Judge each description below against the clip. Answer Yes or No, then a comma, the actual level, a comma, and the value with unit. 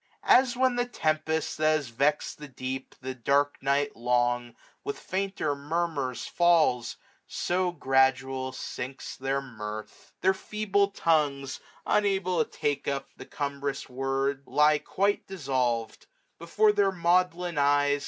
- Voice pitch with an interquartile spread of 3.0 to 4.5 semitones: No, average, 4.9 semitones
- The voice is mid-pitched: Yes, medium, 145 Hz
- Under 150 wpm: Yes, slow, 135 wpm